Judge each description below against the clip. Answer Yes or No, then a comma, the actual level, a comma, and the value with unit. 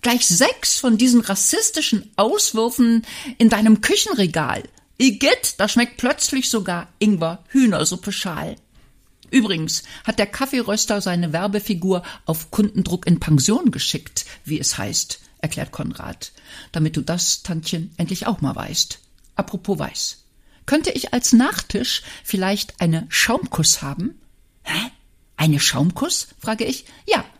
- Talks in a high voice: Yes, high, 205 Hz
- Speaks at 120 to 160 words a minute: Yes, slow, 125 wpm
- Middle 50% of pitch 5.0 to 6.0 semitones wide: Yes, wide, 5.6 semitones